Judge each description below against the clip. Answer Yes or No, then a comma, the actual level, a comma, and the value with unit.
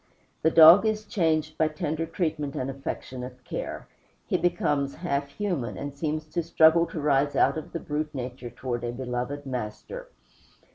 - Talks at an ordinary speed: Yes, average, 160 wpm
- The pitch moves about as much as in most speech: Yes, average, 3.8 semitones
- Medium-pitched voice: Yes, medium, 150 Hz